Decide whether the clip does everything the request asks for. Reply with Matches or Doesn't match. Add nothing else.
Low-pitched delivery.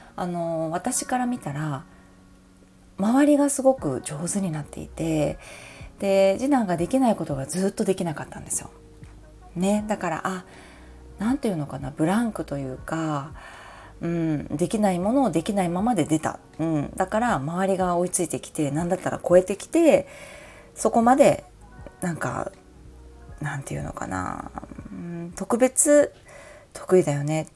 Doesn't match